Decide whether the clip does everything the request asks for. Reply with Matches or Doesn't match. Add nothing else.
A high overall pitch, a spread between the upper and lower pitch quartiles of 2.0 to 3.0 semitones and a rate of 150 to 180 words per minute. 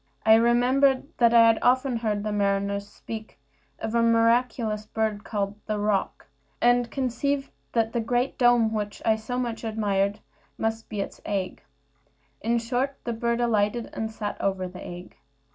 Matches